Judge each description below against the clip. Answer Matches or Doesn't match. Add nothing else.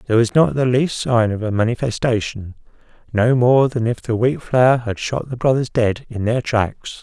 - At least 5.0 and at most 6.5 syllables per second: Doesn't match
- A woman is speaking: Doesn't match